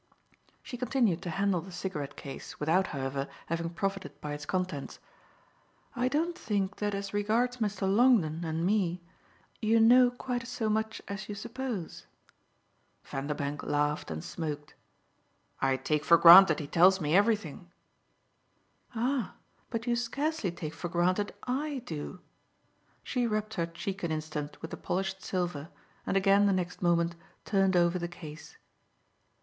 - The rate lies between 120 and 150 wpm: Yes, average, 145 wpm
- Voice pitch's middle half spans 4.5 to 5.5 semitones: Yes, average, 5.2 semitones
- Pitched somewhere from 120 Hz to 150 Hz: No, high, 190 Hz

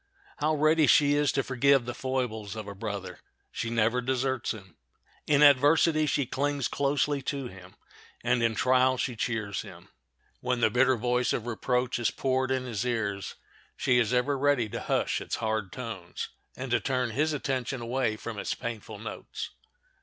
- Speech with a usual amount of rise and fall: Yes, average, 3.3 semitones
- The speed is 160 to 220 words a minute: Yes, average, 175 wpm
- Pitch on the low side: Yes, low, 125 Hz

